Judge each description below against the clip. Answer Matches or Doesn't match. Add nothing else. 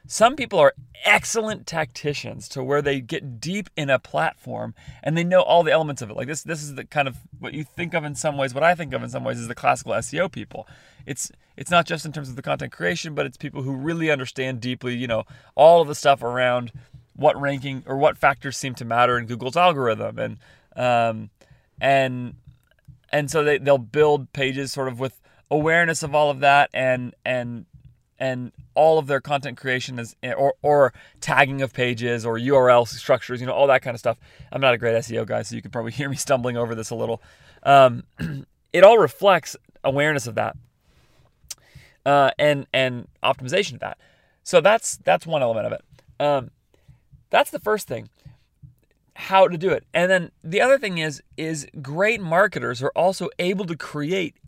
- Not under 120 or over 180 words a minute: Doesn't match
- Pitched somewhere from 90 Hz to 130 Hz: Doesn't match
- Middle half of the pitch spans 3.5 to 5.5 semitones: Matches